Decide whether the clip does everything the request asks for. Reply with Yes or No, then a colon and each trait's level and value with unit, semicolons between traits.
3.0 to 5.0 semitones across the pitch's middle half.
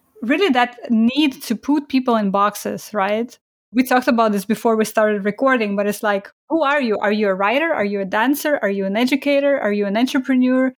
Yes: average, 4.5 semitones